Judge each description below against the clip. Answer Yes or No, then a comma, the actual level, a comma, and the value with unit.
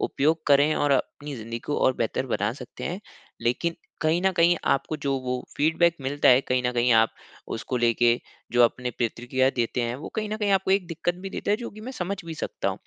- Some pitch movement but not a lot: No, wide, 5.8 semitones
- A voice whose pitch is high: No, medium, 140 Hz